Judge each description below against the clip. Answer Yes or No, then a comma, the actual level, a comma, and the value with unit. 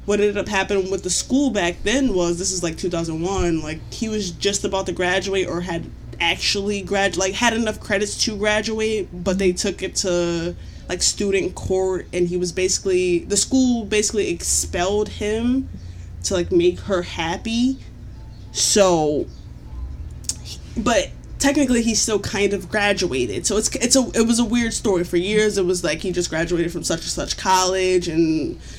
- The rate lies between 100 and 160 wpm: No, average, 175 wpm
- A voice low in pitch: No, high, 190 Hz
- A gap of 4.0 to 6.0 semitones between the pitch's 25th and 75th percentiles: No, average, 3.3 semitones